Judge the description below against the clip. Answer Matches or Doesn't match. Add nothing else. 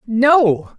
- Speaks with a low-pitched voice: Doesn't match